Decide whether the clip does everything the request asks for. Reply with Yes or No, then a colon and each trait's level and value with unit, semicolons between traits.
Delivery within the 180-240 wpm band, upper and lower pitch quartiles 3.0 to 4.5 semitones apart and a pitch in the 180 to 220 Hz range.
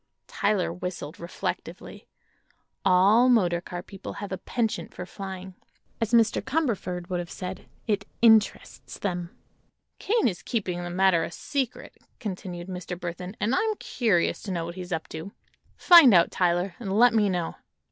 No: average, 155 wpm; average, 3.9 semitones; high, 190 Hz